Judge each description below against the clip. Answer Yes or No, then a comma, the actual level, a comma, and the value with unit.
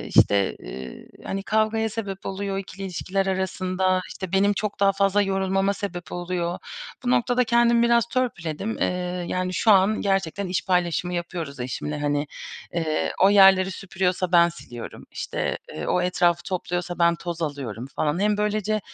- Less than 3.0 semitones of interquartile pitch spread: Yes, narrow, 2.6 semitones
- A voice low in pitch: No, medium, 185 Hz